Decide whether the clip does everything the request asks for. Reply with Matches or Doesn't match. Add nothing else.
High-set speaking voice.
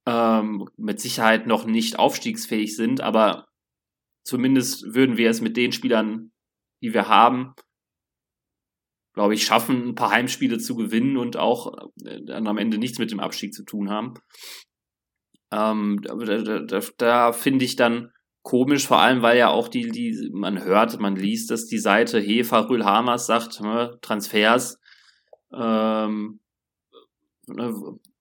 Doesn't match